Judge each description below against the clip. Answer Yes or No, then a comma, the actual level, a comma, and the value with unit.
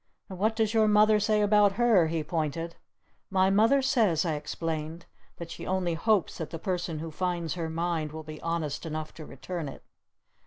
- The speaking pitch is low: No, medium, 170 Hz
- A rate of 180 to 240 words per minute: Yes, average, 190 wpm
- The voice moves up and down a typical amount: Yes, average, 4.5 semitones